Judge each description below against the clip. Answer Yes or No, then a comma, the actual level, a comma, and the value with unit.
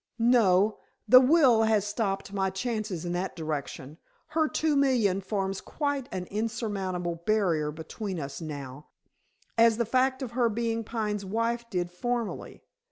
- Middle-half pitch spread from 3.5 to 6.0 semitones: Yes, average, 4.6 semitones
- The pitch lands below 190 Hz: No, high, 210 Hz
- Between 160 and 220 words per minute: No, average, 145 wpm